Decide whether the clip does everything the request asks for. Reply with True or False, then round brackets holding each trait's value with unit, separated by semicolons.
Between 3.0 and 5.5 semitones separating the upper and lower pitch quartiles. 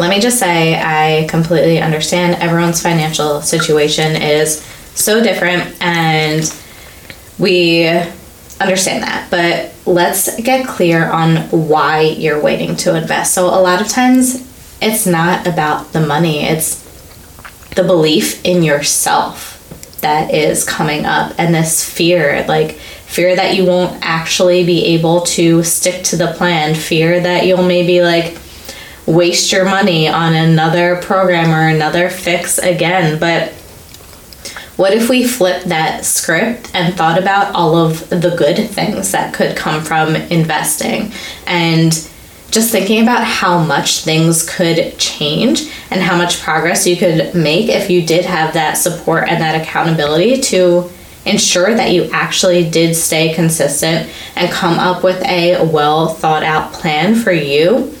False (2.4 semitones)